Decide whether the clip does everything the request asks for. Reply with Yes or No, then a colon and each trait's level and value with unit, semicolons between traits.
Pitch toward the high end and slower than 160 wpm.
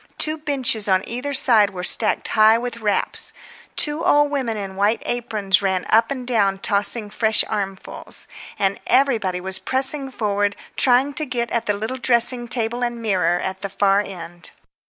No: high, 220 Hz; average, 170 wpm